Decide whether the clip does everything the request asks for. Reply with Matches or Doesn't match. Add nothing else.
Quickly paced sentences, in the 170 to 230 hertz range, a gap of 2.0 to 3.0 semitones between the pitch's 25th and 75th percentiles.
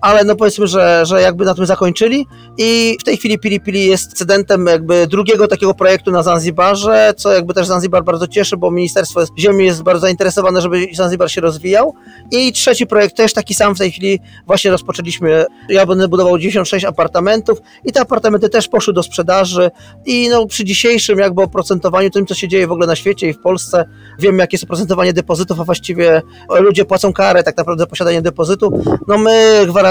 Matches